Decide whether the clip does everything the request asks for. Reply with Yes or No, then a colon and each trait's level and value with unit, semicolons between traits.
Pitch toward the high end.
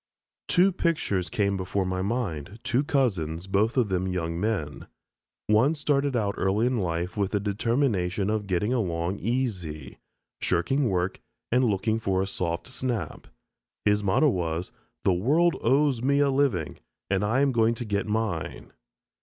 No: low, 105 Hz